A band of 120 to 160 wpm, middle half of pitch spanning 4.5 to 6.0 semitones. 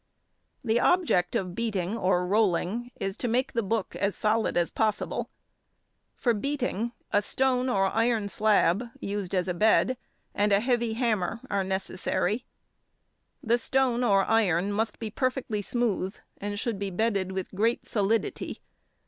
No: average, 150 wpm; average, 3.4 semitones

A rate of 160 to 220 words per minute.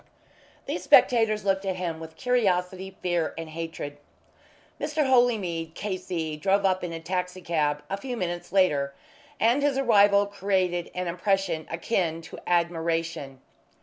No: average, 140 wpm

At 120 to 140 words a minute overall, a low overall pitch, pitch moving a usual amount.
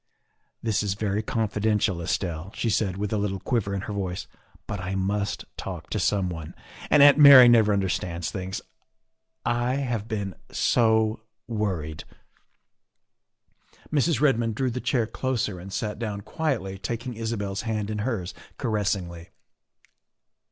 No: average, 150 wpm; low, 105 Hz; average, 3.3 semitones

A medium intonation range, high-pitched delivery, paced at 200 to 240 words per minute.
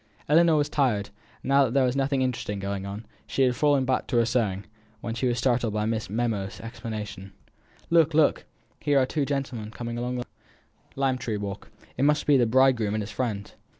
No: average, 3.9 semitones; low, 120 Hz; fast, 205 wpm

